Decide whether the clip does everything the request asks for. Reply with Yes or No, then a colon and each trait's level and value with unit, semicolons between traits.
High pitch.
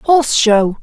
Yes: very high, 250 Hz